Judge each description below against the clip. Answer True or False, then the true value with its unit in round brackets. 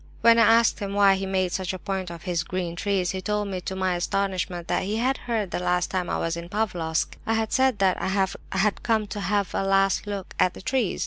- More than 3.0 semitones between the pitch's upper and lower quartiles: False (2.5 semitones)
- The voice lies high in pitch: True (195 Hz)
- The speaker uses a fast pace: True (250 wpm)